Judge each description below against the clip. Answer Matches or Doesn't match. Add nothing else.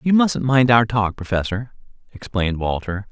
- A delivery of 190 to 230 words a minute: Doesn't match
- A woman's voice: Doesn't match